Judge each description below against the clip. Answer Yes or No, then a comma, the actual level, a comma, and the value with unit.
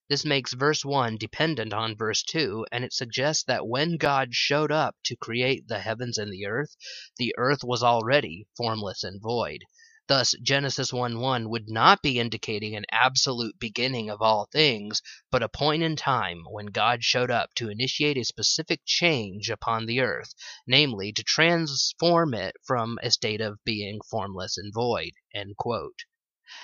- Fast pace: No, average, 160 wpm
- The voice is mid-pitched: No, low, 120 Hz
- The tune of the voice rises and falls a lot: No, average, 4.5 semitones